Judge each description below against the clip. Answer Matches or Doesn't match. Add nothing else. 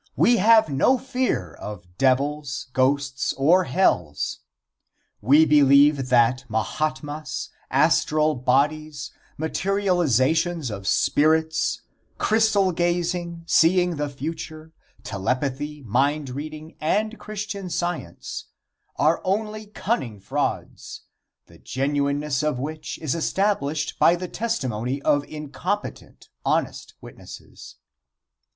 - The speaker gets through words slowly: Matches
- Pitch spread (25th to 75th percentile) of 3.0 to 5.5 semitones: Matches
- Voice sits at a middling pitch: Matches